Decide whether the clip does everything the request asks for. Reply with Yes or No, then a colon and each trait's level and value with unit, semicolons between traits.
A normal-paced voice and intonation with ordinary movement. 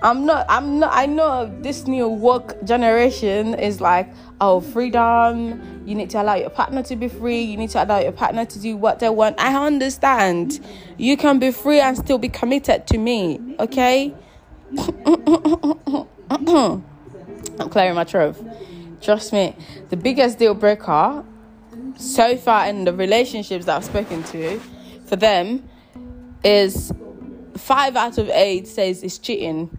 Yes: average, 155 wpm; average, 4.7 semitones